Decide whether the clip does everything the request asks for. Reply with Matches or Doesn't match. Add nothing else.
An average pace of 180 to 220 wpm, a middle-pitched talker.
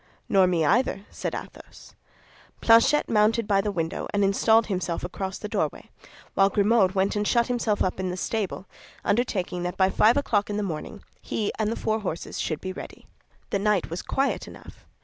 Doesn't match